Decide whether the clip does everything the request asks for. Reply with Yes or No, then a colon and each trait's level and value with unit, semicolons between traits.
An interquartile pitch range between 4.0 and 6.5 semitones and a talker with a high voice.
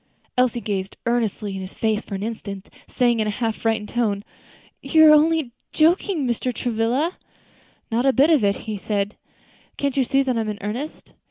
Yes: average, 4.5 semitones; high, 235 Hz